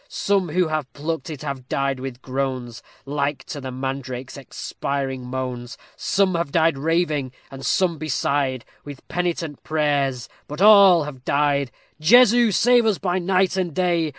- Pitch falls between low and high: Yes, medium, 145 Hz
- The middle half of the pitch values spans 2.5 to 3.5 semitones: No, average, 4.8 semitones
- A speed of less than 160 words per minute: Yes, average, 150 wpm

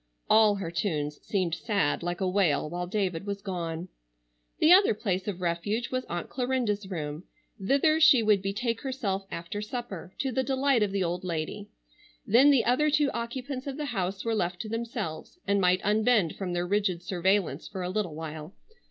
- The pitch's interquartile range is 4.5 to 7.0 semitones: Yes, average, 5.0 semitones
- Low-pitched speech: No, high, 200 Hz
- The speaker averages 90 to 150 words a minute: No, average, 185 wpm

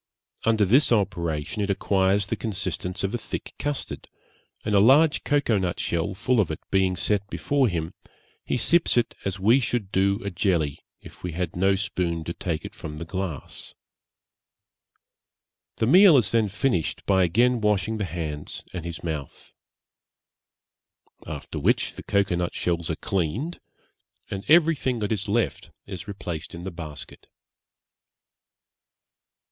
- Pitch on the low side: Yes, very low, 95 Hz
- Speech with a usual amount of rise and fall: Yes, average, 4.6 semitones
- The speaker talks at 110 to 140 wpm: No, average, 150 wpm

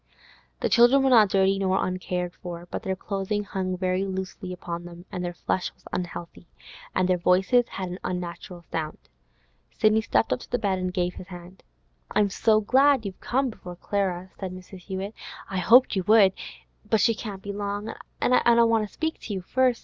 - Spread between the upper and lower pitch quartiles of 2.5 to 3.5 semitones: Yes, average, 3.0 semitones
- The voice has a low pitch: No, high, 190 Hz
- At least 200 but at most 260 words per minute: No, average, 190 wpm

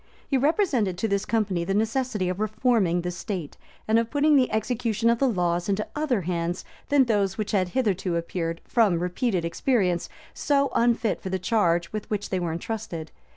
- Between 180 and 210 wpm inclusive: Yes, average, 185 wpm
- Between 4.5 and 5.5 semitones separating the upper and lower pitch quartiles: Yes, average, 4.9 semitones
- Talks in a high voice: Yes, high, 205 Hz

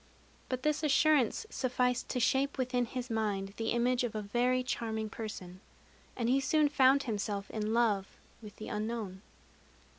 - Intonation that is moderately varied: Yes, average, 3.1 semitones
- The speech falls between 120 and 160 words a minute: Yes, average, 155 wpm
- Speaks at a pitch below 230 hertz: No, high, 240 Hz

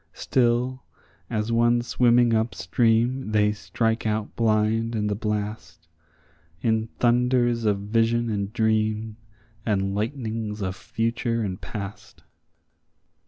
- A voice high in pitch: No, low, 110 Hz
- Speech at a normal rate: No, slow, 115 wpm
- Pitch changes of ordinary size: No, narrow, 2.0 semitones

